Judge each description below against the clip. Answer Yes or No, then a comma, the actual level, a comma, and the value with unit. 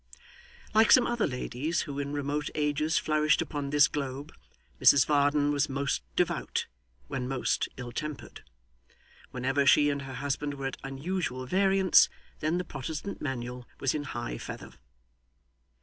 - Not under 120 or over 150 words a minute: Yes, average, 145 wpm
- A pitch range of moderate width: No, narrow, 2.3 semitones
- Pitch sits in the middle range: Yes, medium, 145 Hz